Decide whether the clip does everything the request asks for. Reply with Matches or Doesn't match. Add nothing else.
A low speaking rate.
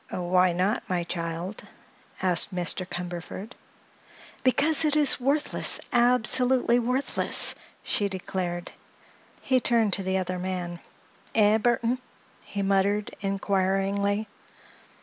Matches